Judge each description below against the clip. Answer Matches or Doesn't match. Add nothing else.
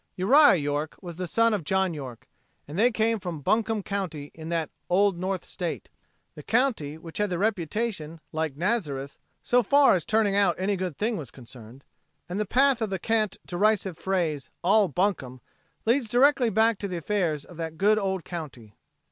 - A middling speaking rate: Matches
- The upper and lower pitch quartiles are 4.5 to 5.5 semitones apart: Matches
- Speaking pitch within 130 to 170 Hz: Doesn't match